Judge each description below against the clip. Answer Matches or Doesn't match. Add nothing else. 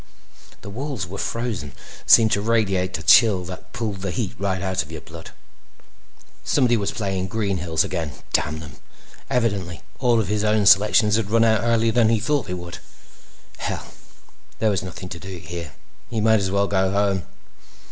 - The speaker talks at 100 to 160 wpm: Doesn't match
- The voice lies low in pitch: Matches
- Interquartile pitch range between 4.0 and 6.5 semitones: Doesn't match